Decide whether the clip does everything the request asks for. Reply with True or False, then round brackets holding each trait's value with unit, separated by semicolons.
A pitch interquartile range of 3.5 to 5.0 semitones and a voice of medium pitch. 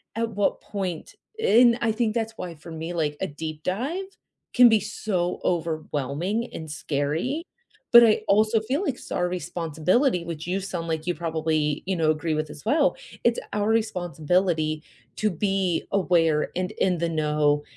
False (5.4 semitones; 175 Hz)